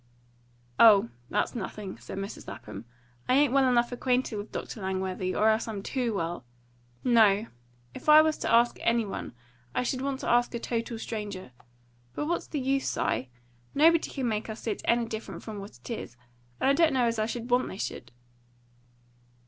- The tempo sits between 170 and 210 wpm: Yes, average, 190 wpm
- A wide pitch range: No, average, 3.8 semitones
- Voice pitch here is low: No, high, 230 Hz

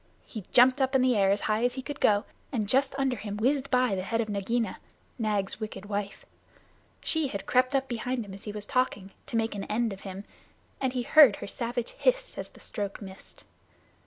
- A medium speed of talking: No, fast, 215 wpm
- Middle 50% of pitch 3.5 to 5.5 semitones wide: Yes, average, 4.0 semitones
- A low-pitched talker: No, high, 230 Hz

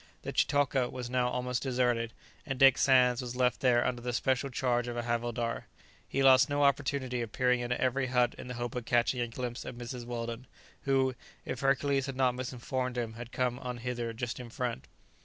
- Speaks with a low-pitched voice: Yes, low, 125 Hz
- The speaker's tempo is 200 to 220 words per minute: Yes, fast, 205 wpm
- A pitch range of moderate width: No, narrow, 1.4 semitones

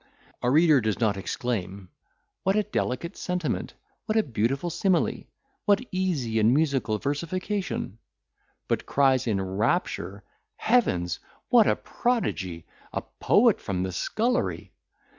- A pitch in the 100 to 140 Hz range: Yes, low, 135 Hz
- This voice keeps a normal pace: No, slow, 120 wpm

